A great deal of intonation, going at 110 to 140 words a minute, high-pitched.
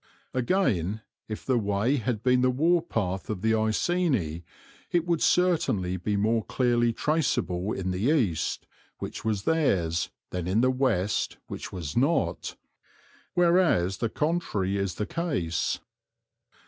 No: wide, 7.7 semitones; slow, 135 wpm; low, 110 Hz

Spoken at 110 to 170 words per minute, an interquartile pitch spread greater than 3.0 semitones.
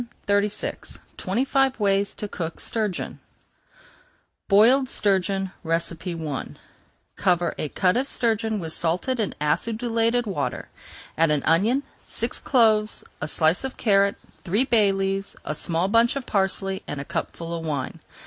Yes: average, 140 wpm; average, 5.1 semitones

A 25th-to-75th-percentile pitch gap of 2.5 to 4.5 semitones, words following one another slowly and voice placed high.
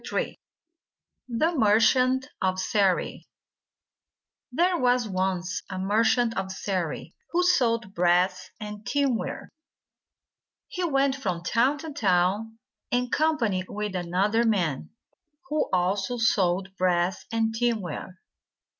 No: average, 4.9 semitones; slow, 110 wpm; high, 210 Hz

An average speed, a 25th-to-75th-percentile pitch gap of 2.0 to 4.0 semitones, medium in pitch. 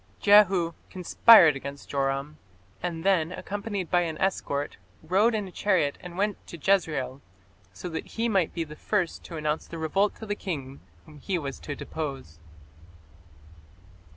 No: average, 155 wpm; average, 4.8 semitones; medium, 170 Hz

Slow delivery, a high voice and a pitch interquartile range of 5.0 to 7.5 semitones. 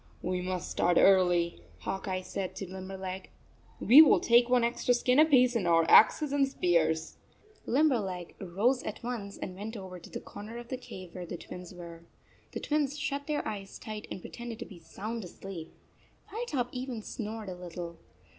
No: average, 185 wpm; high, 200 Hz; wide, 5.4 semitones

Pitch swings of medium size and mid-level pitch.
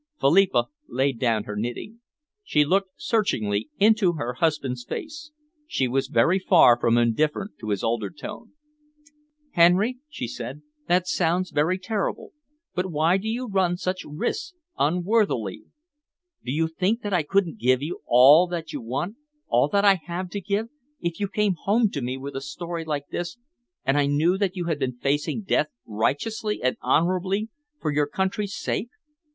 No: wide, 6.3 semitones; medium, 170 Hz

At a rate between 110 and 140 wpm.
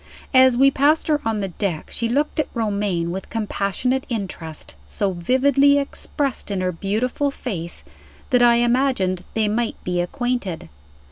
No: average, 150 wpm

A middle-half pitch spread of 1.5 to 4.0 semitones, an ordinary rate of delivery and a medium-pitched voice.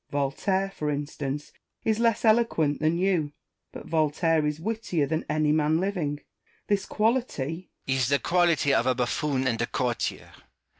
No: average, 4.8 semitones; average, 155 wpm; medium, 155 Hz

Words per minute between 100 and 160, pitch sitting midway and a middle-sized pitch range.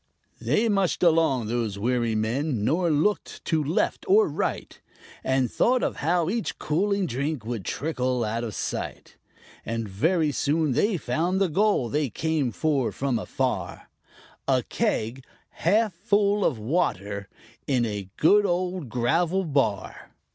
No: average, 140 wpm; medium, 150 Hz; wide, 7.2 semitones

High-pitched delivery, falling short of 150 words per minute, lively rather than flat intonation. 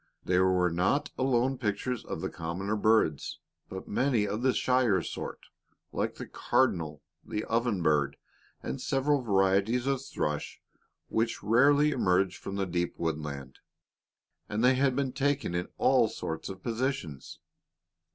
No: low, 105 Hz; average, 140 wpm; wide, 6.4 semitones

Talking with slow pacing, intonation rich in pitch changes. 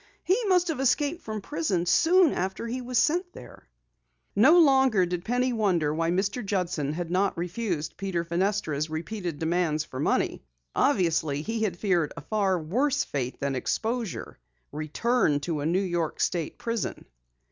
No: average, 160 wpm; wide, 6.8 semitones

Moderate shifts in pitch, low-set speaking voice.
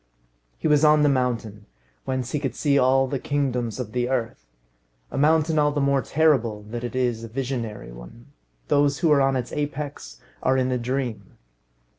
Yes: average, 3.3 semitones; low, 130 Hz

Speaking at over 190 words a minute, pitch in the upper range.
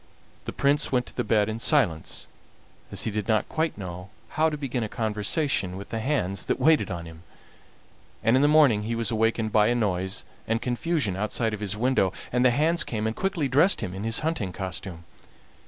No: average, 200 wpm; low, 115 Hz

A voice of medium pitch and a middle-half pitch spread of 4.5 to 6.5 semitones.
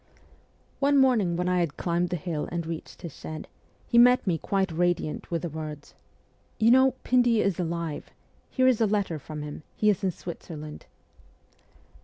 Yes: medium, 175 Hz; average, 5.3 semitones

